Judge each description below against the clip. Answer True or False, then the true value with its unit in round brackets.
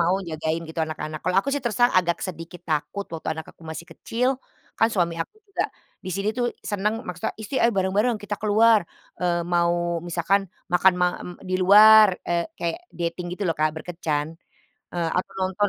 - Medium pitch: True (180 Hz)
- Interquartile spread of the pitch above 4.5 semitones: False (3.6 semitones)